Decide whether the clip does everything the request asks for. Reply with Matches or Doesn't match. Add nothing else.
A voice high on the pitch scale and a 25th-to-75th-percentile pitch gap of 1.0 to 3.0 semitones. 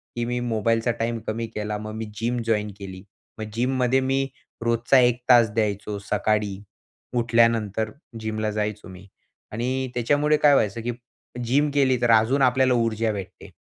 Doesn't match